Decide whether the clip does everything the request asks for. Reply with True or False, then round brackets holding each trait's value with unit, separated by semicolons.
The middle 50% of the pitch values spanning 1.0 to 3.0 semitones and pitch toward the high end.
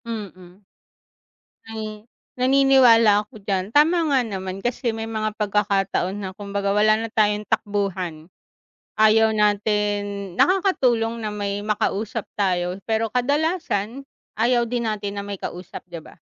True (2.4 semitones; 210 Hz)